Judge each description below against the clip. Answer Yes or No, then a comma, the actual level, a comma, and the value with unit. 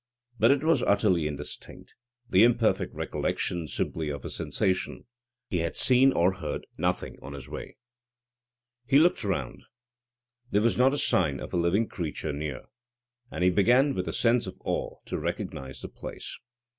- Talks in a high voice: No, very low, 95 Hz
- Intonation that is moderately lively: No, wide, 7.0 semitones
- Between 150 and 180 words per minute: Yes, average, 165 wpm